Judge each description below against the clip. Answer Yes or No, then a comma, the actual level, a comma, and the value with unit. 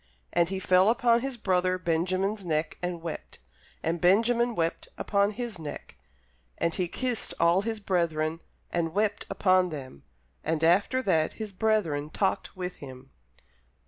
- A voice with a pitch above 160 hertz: Yes, medium, 185 Hz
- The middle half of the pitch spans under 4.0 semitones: No, average, 4.4 semitones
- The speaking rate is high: No, average, 145 wpm